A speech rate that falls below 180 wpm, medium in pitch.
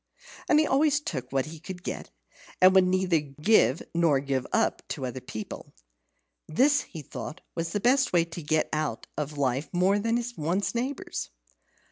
Yes: average, 160 wpm; medium, 170 Hz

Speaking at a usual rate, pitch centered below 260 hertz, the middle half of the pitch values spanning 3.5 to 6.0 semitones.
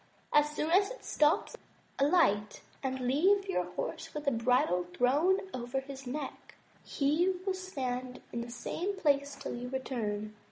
No: average, 155 wpm; very high, 275 Hz; average, 5.1 semitones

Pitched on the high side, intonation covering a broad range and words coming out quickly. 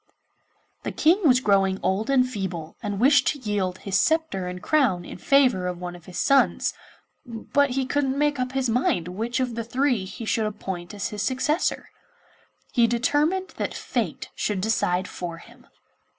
No: high, 230 Hz; wide, 6.1 semitones; average, 175 wpm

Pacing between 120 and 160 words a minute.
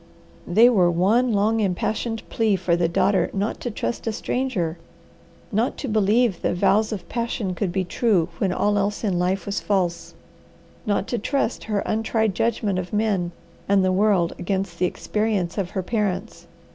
No: average, 170 wpm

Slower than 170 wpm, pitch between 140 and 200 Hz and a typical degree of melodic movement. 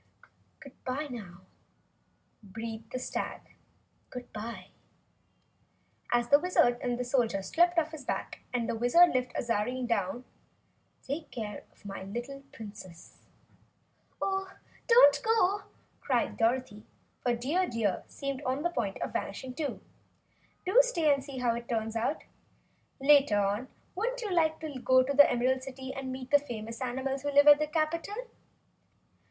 No: average, 145 wpm; very high, 260 Hz; average, 4.4 semitones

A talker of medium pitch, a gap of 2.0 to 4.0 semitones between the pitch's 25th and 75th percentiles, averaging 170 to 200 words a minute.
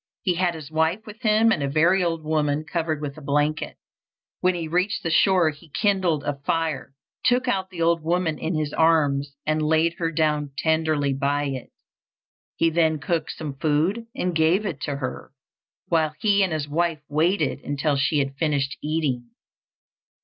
Yes: medium, 160 Hz; average, 2.8 semitones; average, 180 wpm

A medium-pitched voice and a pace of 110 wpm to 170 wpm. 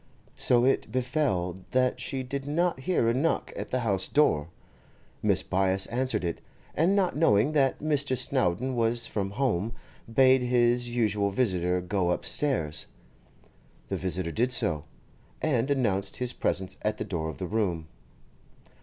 No: low, 120 Hz; average, 150 wpm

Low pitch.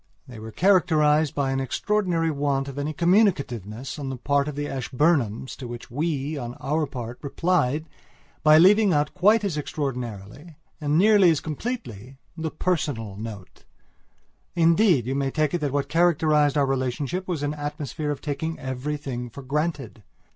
No: medium, 145 Hz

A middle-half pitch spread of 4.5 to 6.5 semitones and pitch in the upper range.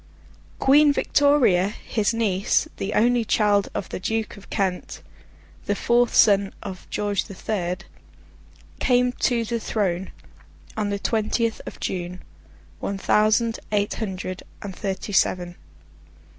No: average, 3.1 semitones; high, 205 Hz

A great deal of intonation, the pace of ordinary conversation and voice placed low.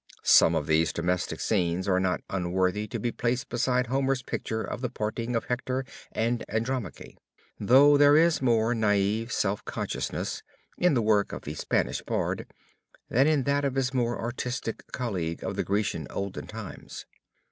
No: average, 4.6 semitones; average, 165 wpm; low, 115 Hz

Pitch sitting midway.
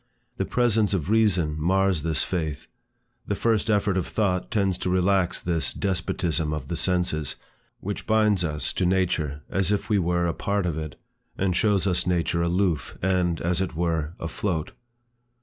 No: very low, 90 Hz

